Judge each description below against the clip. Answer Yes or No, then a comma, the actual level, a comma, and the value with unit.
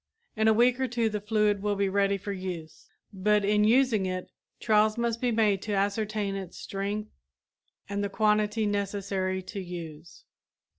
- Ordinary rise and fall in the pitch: No, narrow, 1.8 semitones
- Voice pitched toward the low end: No, high, 205 Hz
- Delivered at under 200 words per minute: Yes, average, 165 wpm